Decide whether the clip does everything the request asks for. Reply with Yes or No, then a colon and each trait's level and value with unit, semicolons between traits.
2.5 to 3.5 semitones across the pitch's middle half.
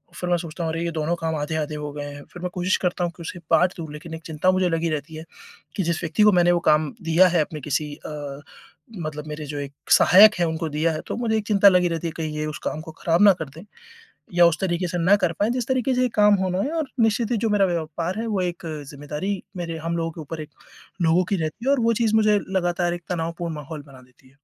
Yes: average, 3.1 semitones